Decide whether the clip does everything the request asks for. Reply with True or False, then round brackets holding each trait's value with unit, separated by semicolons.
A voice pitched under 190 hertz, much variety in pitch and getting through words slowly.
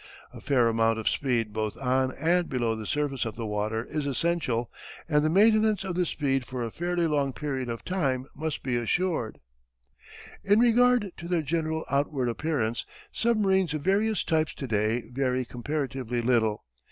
False (140 Hz; 6.2 semitones; 170 wpm)